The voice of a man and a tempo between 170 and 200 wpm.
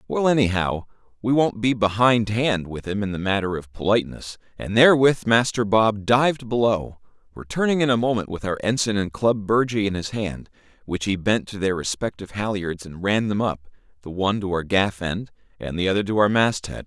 Yes: male; average, 195 wpm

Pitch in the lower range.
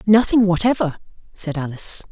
No: medium, 185 Hz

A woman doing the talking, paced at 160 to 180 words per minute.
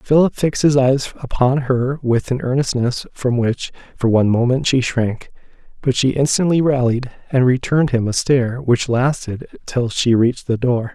No: male; average, 175 wpm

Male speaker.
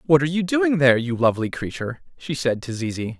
Yes: male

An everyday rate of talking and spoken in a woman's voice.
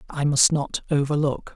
No: average, 155 wpm; male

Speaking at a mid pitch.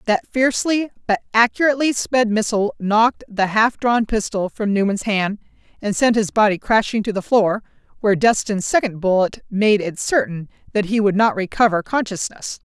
No: high, 215 Hz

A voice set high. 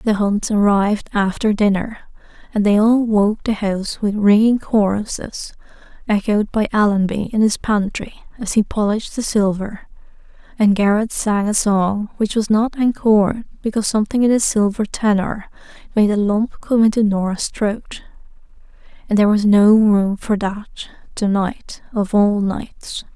Yes: high, 210 Hz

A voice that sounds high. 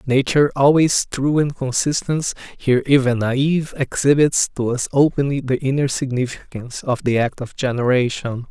No: low, 135 Hz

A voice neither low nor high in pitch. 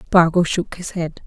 Yes: medium, 170 Hz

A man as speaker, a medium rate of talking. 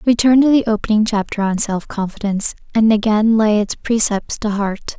No: female; average, 180 wpm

